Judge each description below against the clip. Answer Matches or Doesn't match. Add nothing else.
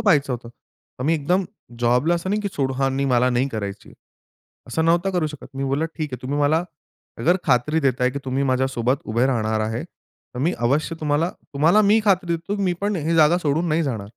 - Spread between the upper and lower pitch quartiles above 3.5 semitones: Matches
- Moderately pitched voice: Matches